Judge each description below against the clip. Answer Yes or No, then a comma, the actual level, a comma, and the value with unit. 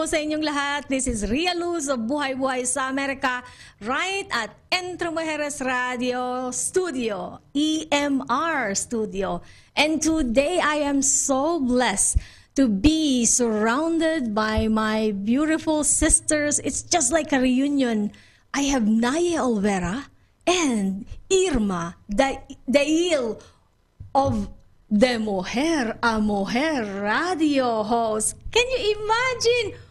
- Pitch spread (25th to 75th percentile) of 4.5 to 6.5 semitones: Yes, average, 5.3 semitones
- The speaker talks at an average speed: No, slow, 110 wpm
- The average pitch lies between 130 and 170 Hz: No, very high, 270 Hz